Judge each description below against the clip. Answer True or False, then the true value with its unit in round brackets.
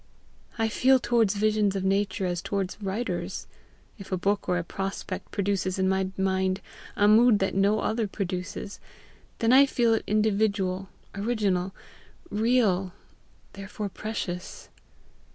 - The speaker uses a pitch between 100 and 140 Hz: False (200 Hz)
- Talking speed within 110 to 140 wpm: True (135 wpm)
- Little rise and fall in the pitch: True (2.3 semitones)